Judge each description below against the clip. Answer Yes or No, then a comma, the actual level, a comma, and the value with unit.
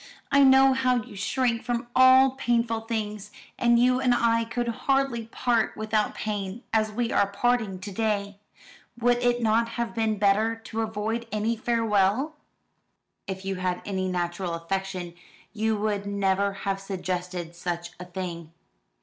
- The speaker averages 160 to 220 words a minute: No, average, 150 wpm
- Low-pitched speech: No, high, 215 Hz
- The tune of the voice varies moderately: Yes, average, 3.5 semitones